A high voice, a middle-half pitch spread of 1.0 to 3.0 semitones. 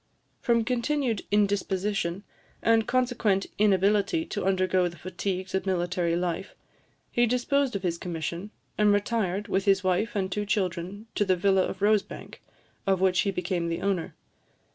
Yes: high, 195 Hz; narrow, 2.6 semitones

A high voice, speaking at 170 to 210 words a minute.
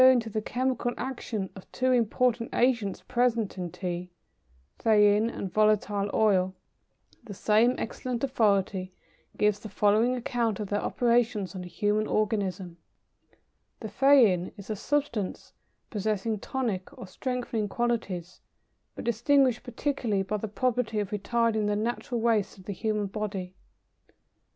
No: high, 215 Hz; average, 140 wpm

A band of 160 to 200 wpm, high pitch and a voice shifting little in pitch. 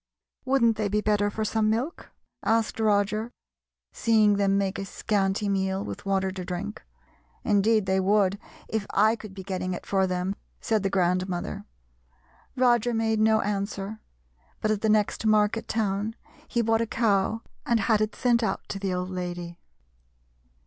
Yes: average, 165 wpm; high, 205 Hz; narrow, 2.3 semitones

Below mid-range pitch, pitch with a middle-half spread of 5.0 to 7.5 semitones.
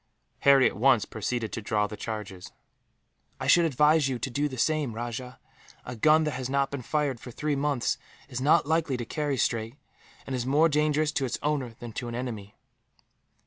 No: low, 130 Hz; average, 4.0 semitones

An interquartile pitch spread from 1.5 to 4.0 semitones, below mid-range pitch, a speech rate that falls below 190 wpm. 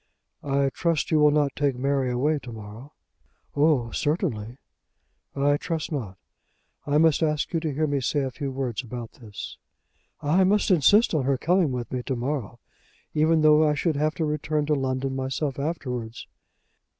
No: average, 3.0 semitones; medium, 145 Hz; average, 175 wpm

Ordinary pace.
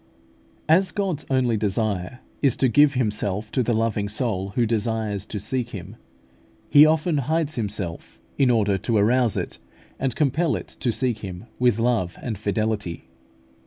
Yes: average, 160 wpm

